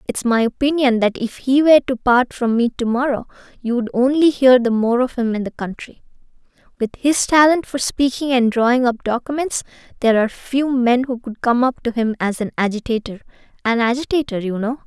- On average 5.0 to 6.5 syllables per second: Yes, 5.4 syllables/s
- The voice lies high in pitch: Yes, high, 245 Hz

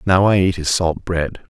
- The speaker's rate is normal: No, fast, 225 wpm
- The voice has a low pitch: Yes, very low, 90 Hz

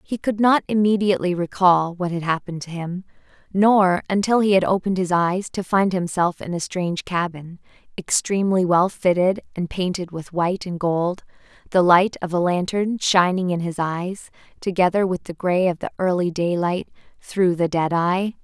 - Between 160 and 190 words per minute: Yes, average, 175 wpm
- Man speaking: No, female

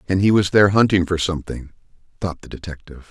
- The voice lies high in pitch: No, very low, 90 Hz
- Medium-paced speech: Yes, average, 195 wpm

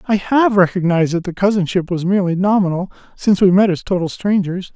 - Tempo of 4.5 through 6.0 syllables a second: No, 6.2 syllables/s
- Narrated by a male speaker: Yes, male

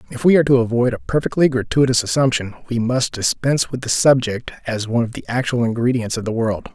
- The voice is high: No, low, 120 Hz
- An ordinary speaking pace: No, fast, 215 wpm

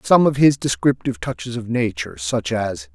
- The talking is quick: No, average, 185 wpm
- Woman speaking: No, male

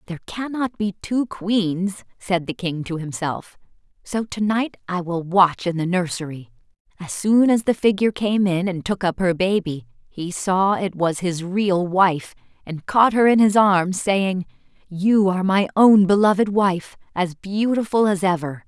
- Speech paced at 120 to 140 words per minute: No, average, 175 wpm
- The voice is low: No, high, 190 Hz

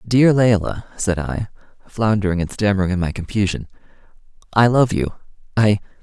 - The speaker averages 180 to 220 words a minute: No, average, 140 wpm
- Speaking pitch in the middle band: No, low, 100 Hz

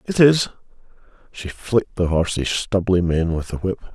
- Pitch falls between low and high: No, very low, 95 Hz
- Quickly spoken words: No, average, 165 wpm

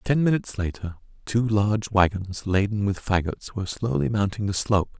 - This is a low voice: Yes, low, 100 Hz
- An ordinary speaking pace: Yes, average, 170 wpm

